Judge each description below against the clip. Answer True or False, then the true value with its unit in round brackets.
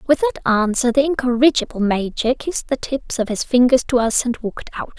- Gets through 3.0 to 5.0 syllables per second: False (5.8 syllables/s)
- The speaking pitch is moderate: False (250 Hz)